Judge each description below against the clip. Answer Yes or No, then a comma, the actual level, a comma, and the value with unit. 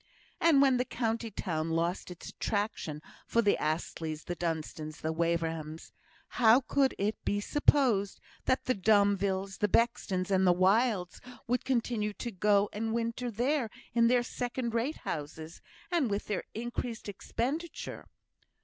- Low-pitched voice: No, high, 210 Hz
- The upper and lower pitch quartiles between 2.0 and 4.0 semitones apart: No, average, 5.2 semitones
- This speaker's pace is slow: No, average, 145 wpm